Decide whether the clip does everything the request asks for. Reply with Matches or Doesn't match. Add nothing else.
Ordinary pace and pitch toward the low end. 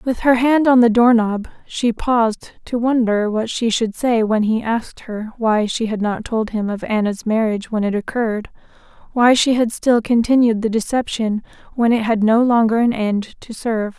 Doesn't match